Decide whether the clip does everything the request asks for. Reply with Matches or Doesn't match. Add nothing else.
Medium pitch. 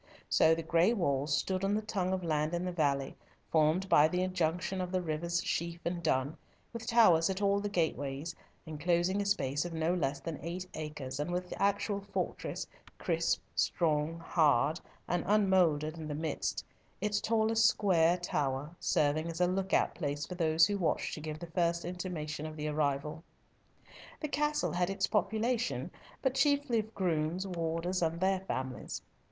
Matches